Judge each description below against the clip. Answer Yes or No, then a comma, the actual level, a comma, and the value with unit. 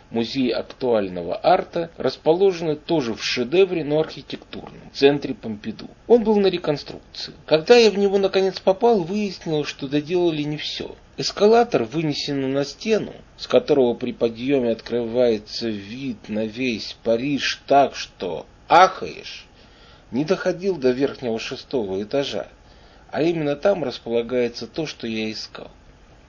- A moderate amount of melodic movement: No, wide, 7.1 semitones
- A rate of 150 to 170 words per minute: No, average, 130 wpm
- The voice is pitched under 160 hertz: Yes, medium, 140 Hz